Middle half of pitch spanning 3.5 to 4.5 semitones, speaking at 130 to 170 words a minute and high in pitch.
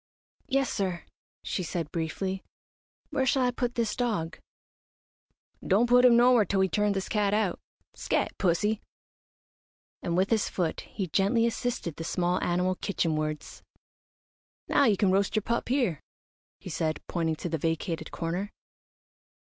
No: average, 5.0 semitones; average, 150 wpm; high, 195 Hz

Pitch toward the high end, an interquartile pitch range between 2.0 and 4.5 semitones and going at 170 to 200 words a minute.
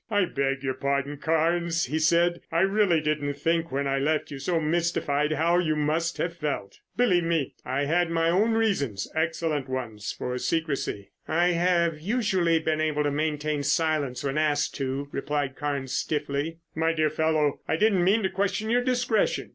No: medium, 155 Hz; average, 3.2 semitones; average, 175 wpm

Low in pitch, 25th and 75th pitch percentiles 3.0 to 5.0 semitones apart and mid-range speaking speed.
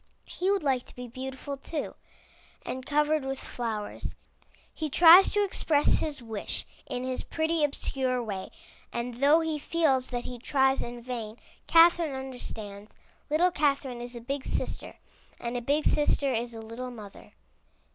No: very high, 265 Hz; average, 3.9 semitones; average, 155 wpm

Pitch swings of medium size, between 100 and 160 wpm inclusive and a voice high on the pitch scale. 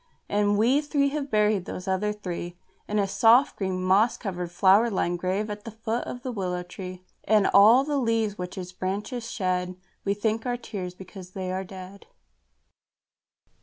No: average, 3.4 semitones; average, 175 wpm; high, 200 Hz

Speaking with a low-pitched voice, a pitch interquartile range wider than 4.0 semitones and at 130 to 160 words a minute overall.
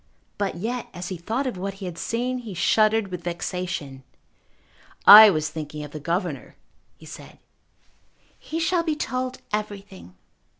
No: high, 195 Hz; average, 5.1 semitones; average, 155 wpm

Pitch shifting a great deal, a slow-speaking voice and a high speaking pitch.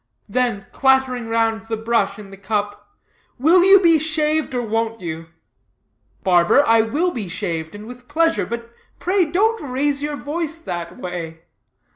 No: wide, 6.9 semitones; average, 155 wpm; high, 235 Hz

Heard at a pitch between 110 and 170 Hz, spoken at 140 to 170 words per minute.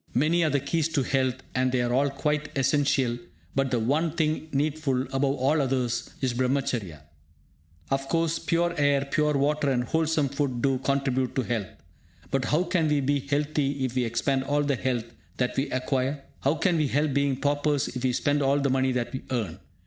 No: medium, 140 Hz; average, 195 wpm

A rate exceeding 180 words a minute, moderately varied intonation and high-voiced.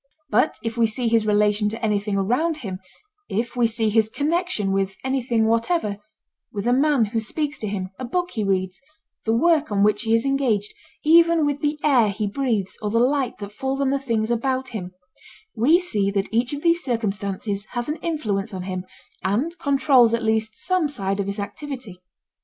Yes: average, 190 wpm; average, 5.0 semitones; high, 230 Hz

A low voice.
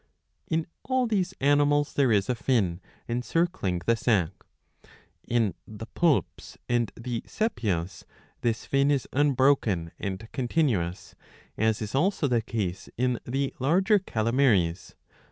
Yes: low, 120 Hz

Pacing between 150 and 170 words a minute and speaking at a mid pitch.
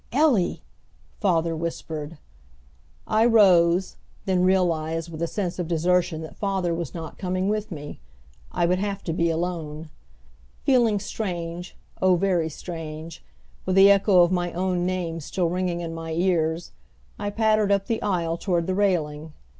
Yes: average, 155 wpm; medium, 175 Hz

